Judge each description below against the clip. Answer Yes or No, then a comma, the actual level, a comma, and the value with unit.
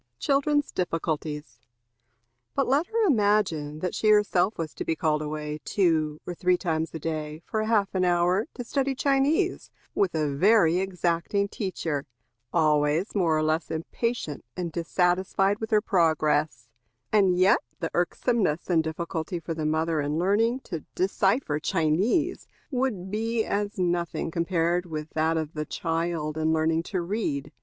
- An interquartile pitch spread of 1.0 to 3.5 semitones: No, average, 4.5 semitones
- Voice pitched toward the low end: No, medium, 175 Hz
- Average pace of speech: Yes, average, 150 wpm